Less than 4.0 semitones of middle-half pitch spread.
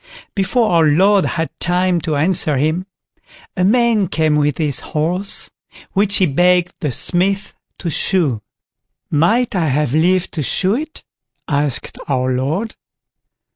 No: average, 4.4 semitones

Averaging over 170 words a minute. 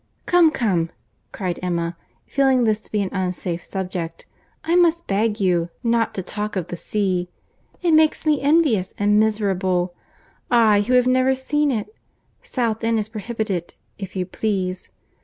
No: average, 155 wpm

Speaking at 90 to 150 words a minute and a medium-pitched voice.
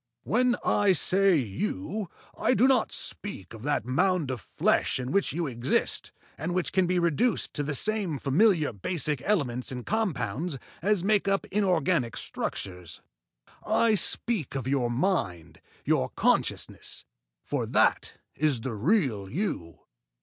Yes: average, 140 wpm; medium, 155 Hz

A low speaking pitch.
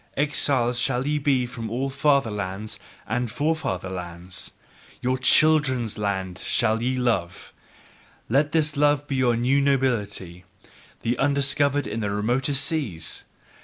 Yes: low, 125 Hz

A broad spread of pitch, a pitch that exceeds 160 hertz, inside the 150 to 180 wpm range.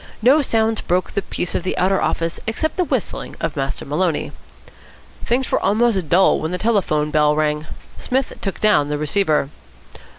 Yes: wide, 6.5 semitones; high, 190 Hz; average, 170 wpm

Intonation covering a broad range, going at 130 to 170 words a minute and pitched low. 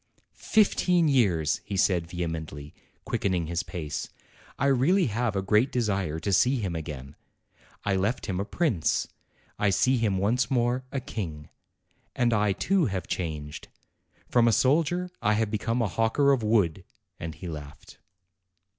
Yes: wide, 6.5 semitones; average, 155 wpm; low, 105 Hz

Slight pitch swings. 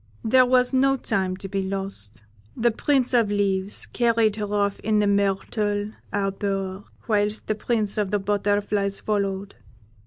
Yes: narrow, 1.8 semitones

